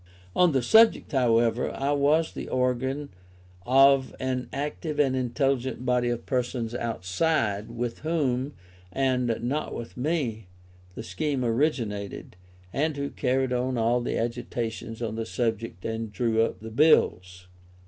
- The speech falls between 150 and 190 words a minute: No, average, 140 wpm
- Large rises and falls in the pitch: No, average, 3.3 semitones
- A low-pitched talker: Yes, low, 125 Hz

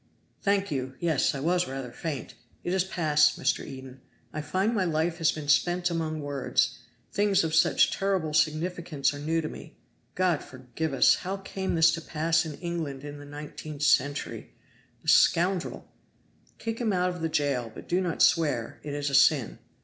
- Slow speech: No, average, 180 wpm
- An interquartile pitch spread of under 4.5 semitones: Yes, average, 3.5 semitones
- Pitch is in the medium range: Yes, medium, 160 Hz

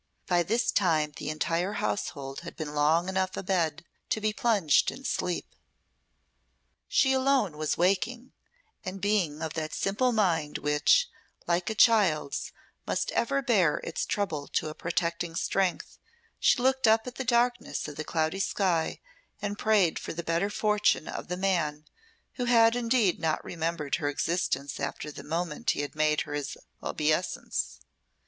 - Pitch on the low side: No, medium, 175 Hz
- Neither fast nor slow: Yes, average, 155 wpm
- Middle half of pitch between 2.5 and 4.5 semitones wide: No, wide, 5.6 semitones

